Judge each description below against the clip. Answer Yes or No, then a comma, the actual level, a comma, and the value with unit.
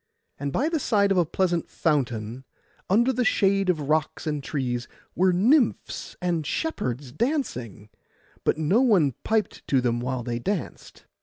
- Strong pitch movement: Yes, wide, 8.1 semitones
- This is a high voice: No, medium, 160 Hz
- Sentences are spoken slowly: No, average, 155 wpm